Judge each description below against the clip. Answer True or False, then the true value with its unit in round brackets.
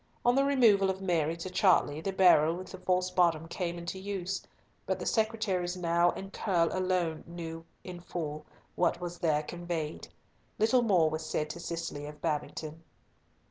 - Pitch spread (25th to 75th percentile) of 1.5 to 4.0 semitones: True (2.6 semitones)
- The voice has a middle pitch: True (175 Hz)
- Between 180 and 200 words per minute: False (170 wpm)